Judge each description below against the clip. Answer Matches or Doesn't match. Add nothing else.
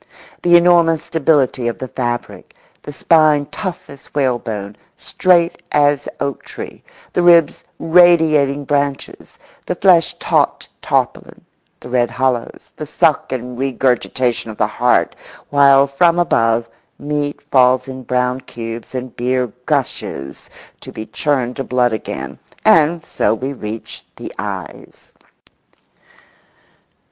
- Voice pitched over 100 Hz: Matches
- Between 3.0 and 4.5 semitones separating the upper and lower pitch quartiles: Matches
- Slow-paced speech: Matches